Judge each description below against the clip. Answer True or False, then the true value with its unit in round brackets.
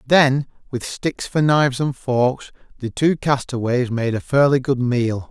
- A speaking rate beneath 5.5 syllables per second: True (4.1 syllables/s)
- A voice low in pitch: True (130 Hz)